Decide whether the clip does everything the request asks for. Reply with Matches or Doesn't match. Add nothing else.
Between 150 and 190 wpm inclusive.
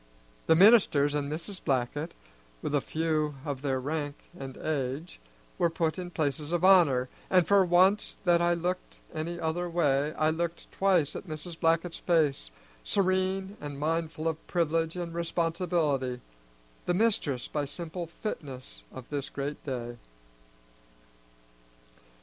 Doesn't match